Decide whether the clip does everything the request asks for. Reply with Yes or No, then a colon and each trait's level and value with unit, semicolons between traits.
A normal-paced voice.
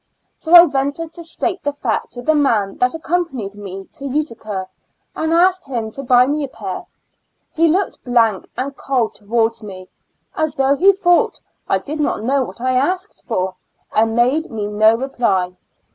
Yes: average, 185 wpm